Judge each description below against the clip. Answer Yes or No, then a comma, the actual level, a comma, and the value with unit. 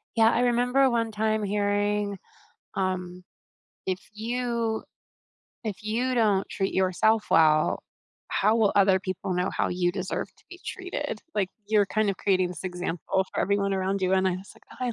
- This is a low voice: No, high, 200 Hz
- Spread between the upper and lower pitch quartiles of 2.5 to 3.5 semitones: Yes, average, 2.9 semitones